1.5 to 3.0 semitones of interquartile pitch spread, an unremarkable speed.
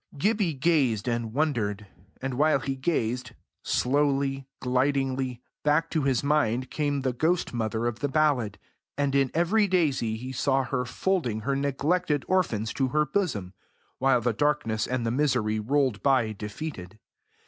No: average, 4.0 semitones; average, 150 wpm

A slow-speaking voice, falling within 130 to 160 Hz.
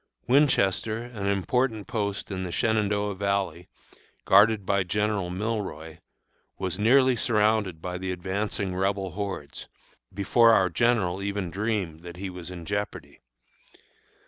No: slow, 125 wpm; low, 100 Hz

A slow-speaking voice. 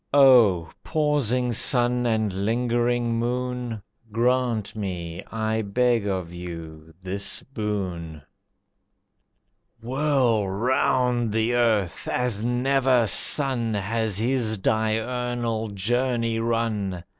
Yes: slow, 90 wpm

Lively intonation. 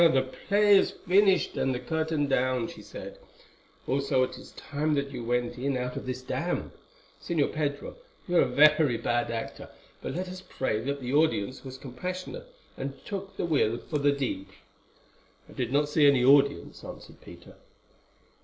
No: average, 3.9 semitones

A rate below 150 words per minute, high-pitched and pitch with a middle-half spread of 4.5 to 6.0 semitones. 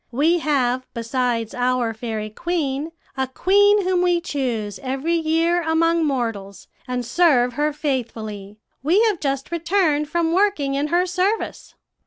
Yes: average, 140 wpm; very high, 290 Hz; wide, 5.6 semitones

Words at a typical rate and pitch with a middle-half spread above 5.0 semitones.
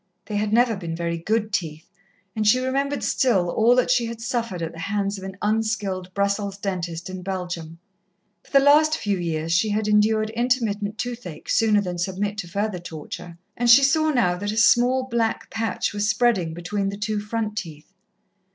No: average, 190 wpm; average, 4.2 semitones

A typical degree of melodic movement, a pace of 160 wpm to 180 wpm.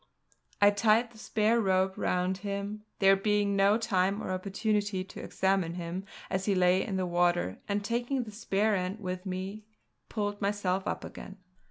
No: narrow, 2.1 semitones; average, 170 wpm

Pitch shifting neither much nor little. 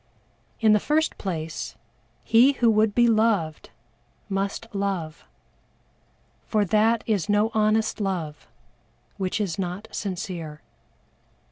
Yes: average, 3.4 semitones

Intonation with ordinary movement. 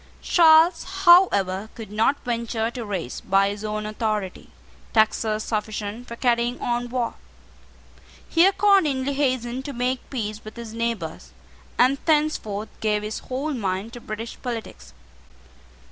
Yes: average, 3.5 semitones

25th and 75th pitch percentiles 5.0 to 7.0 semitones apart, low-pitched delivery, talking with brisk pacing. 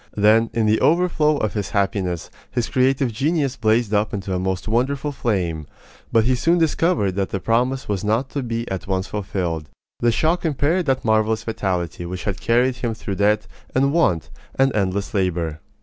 No: wide, 5.4 semitones; low, 110 Hz; average, 180 wpm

